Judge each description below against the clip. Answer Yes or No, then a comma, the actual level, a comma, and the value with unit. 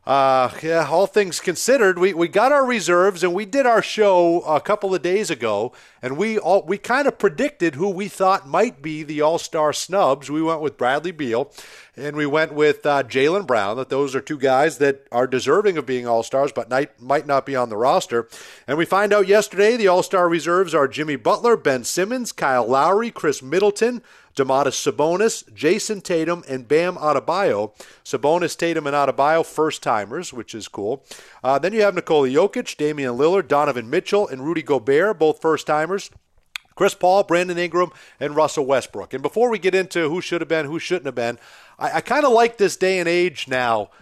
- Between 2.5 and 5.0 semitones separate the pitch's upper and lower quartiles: No, wide, 5.5 semitones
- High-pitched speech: No, medium, 170 Hz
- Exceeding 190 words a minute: Yes, average, 200 wpm